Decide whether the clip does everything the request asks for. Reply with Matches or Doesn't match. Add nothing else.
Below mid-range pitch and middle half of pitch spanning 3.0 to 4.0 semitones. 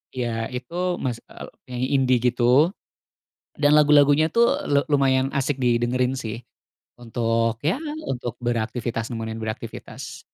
Matches